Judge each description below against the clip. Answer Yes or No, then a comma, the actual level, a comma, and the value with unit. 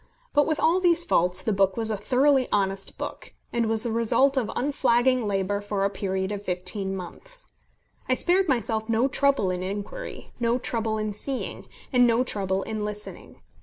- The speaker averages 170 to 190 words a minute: Yes, average, 180 wpm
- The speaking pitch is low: No, high, 220 Hz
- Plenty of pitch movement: No, average, 4.8 semitones